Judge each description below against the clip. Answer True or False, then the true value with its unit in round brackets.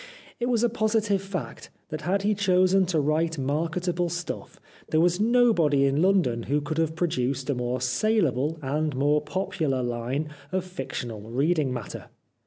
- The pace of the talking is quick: False (175 wpm)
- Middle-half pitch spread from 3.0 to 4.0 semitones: False (5.3 semitones)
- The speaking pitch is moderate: True (160 Hz)